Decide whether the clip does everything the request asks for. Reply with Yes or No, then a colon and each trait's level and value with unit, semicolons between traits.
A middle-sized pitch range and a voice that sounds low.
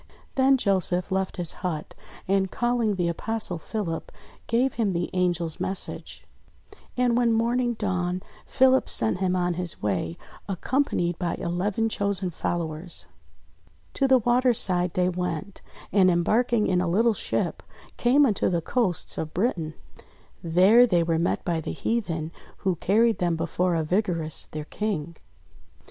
No: average, 4.8 semitones; medium, 185 Hz